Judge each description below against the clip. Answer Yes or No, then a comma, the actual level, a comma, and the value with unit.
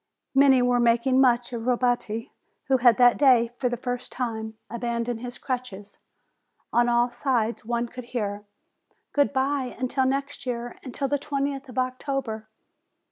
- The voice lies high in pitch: Yes, high, 245 Hz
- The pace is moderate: Yes, average, 150 wpm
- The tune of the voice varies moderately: No, narrow, 1.9 semitones